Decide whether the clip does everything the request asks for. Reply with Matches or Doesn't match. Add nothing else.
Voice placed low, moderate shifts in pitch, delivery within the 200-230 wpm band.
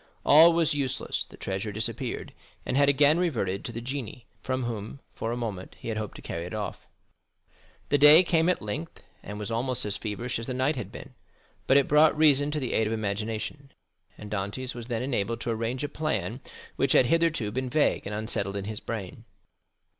Matches